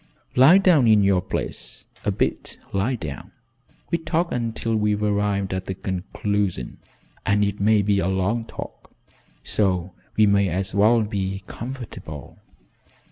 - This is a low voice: Yes, low, 100 Hz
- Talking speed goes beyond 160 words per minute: No, average, 140 wpm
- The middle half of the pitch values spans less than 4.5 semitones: Yes, average, 2.9 semitones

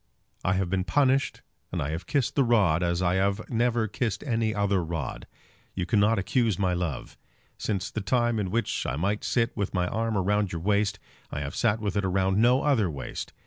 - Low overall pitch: Yes, low, 100 Hz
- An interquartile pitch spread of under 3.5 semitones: No, average, 3.9 semitones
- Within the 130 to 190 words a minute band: No, average, 200 wpm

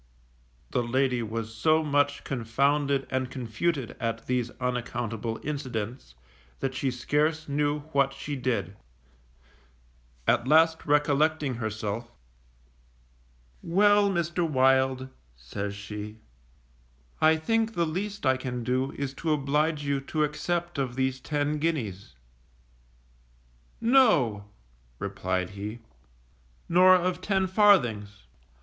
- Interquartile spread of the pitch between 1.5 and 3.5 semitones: No, average, 5.0 semitones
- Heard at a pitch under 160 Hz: Yes, low, 135 Hz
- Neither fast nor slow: No, slow, 110 wpm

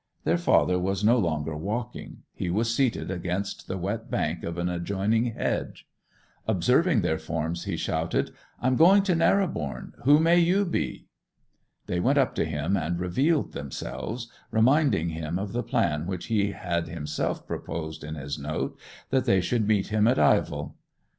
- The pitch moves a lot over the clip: Yes, wide, 6.7 semitones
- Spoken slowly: No, average, 165 wpm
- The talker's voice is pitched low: Yes, very low, 95 Hz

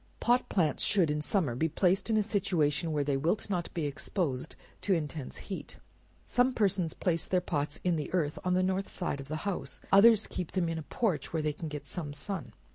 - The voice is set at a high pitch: No, medium, 170 Hz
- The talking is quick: Yes, fast, 215 wpm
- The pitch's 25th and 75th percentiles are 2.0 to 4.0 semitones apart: No, average, 4.6 semitones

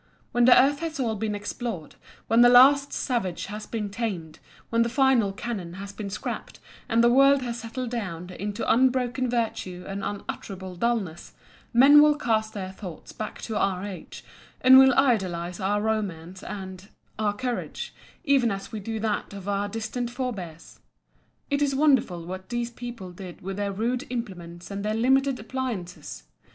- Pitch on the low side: No, high, 220 Hz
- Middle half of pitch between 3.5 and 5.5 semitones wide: Yes, average, 4.3 semitones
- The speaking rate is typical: Yes, average, 165 wpm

